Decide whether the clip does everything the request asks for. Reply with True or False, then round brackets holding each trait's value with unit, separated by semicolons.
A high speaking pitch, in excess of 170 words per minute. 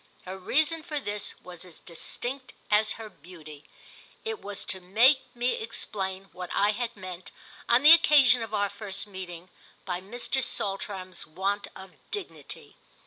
False (205 Hz; 150 wpm)